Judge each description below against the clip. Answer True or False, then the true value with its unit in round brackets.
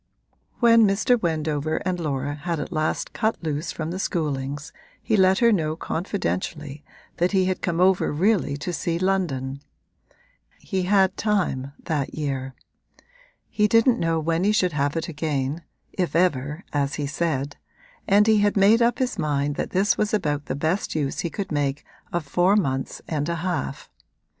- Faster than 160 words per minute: True (170 wpm)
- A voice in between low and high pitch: True (165 Hz)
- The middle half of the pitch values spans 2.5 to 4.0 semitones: False (4.7 semitones)